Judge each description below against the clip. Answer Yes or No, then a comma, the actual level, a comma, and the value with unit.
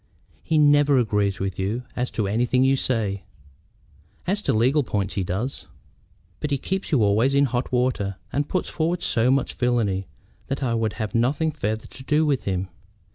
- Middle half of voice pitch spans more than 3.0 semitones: Yes, average, 5.2 semitones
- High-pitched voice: No, low, 125 Hz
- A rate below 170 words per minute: No, average, 185 wpm